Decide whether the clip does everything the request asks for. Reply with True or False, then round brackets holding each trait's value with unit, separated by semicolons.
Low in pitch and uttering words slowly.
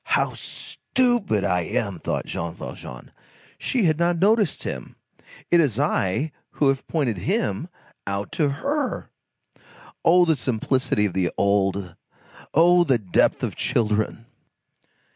True (130 Hz; 125 wpm)